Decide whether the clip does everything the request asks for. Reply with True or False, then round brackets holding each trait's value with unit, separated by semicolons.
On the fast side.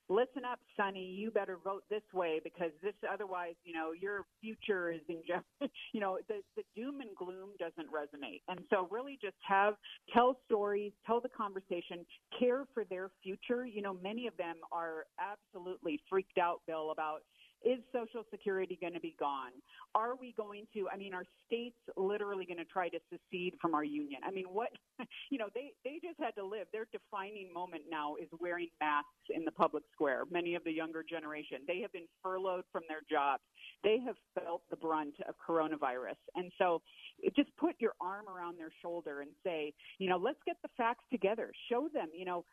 False (195 wpm)